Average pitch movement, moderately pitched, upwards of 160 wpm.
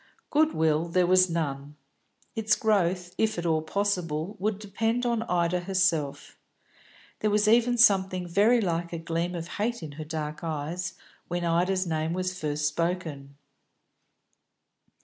No: average, 4.0 semitones; medium, 175 Hz; average, 145 wpm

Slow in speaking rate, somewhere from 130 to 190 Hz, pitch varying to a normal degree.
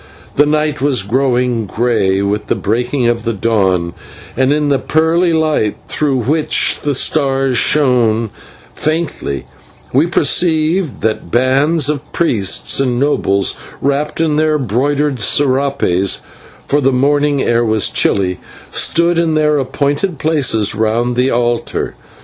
Yes: slow, 130 wpm; low, 135 Hz; average, 4.6 semitones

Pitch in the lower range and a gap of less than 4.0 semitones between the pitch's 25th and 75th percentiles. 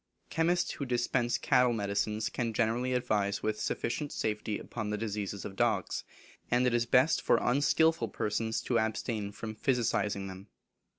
Yes: low, 115 Hz; average, 2.9 semitones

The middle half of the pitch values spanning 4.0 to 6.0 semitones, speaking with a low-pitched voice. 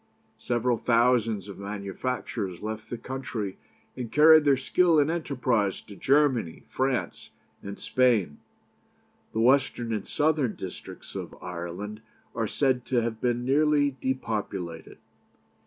Yes: average, 4.3 semitones; low, 120 Hz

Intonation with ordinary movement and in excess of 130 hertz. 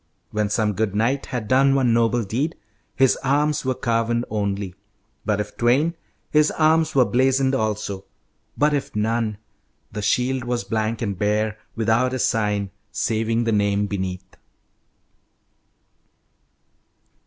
No: average, 3.8 semitones; low, 115 Hz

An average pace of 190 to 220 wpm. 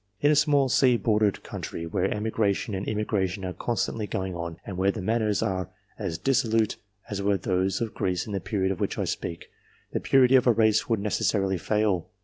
Yes: fast, 205 wpm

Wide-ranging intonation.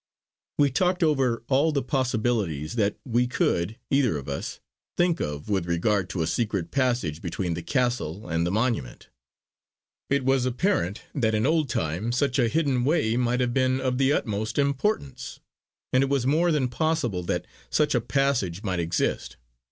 Yes: wide, 6.3 semitones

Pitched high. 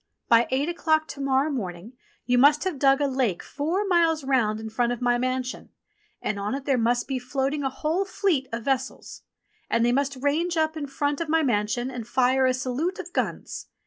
Yes: very high, 265 Hz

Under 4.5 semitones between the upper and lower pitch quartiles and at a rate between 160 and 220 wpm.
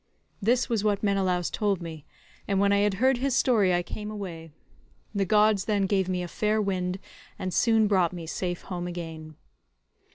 Yes: average, 3.1 semitones; average, 185 wpm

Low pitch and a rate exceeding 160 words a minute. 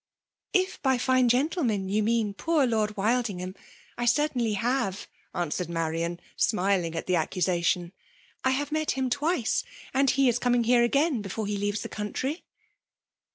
No: high, 230 Hz; average, 180 wpm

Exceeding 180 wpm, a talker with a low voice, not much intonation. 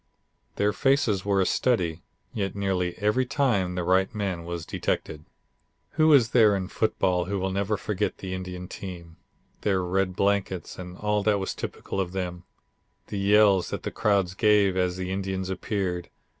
No: average, 170 wpm; very low, 95 Hz; narrow, 2.2 semitones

